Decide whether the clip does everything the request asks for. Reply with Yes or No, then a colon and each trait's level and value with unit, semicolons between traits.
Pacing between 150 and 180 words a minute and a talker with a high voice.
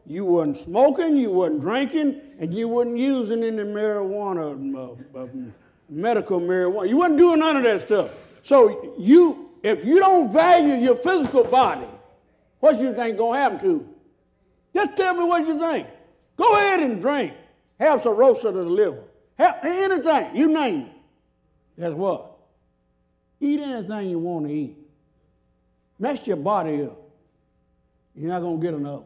Yes: average, 160 wpm; high, 235 Hz